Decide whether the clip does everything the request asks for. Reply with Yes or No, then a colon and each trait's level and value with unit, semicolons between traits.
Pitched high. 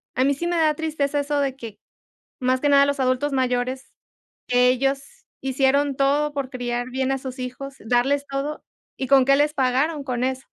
Yes: very high, 270 Hz